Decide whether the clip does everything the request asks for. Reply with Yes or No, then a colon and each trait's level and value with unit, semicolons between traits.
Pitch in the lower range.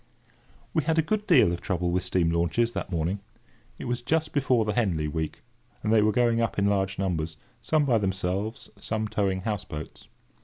Yes: low, 100 Hz